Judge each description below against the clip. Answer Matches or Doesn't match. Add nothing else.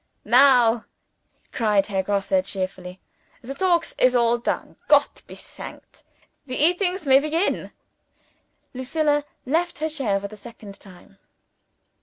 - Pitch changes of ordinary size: Doesn't match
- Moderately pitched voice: Doesn't match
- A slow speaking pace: Matches